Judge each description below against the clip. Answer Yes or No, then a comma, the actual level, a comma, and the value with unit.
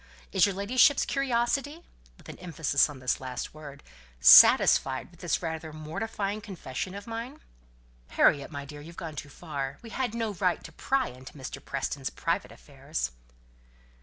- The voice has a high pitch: No, medium, 165 Hz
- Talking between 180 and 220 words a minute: No, average, 160 wpm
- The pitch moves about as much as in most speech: No, wide, 7.9 semitones